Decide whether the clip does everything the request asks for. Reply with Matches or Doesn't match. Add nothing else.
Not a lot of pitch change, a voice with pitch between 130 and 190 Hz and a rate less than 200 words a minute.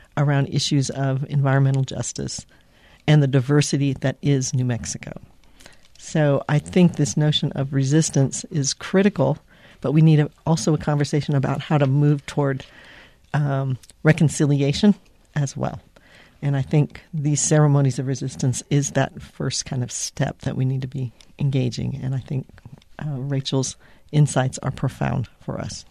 Matches